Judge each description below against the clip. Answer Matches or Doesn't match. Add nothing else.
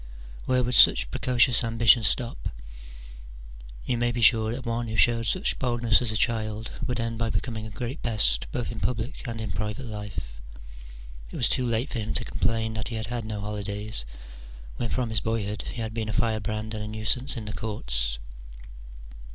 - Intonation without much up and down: Matches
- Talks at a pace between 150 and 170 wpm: Doesn't match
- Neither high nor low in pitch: Doesn't match